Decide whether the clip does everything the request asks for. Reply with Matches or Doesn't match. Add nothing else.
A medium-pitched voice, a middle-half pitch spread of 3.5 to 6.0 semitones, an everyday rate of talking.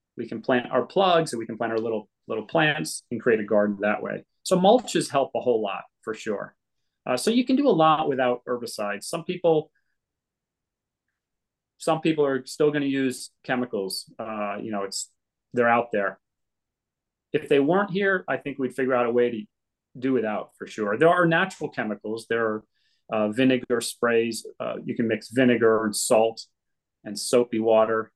Doesn't match